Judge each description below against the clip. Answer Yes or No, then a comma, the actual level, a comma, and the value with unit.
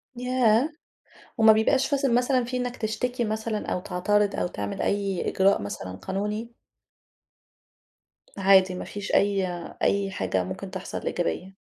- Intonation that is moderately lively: Yes, average, 4.0 semitones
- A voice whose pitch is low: No, high, 205 Hz